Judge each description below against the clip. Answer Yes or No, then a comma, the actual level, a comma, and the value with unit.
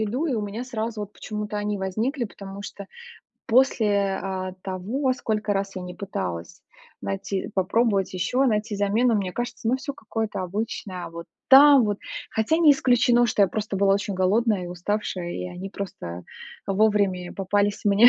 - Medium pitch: No, high, 205 Hz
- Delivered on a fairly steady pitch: No, average, 3.1 semitones